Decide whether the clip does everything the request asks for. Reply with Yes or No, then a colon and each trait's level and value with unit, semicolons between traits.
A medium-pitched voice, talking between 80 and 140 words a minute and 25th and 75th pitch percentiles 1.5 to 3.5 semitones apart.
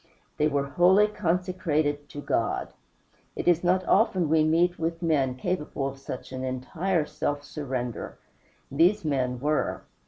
No: medium, 155 Hz; slow, 135 wpm; average, 4.2 semitones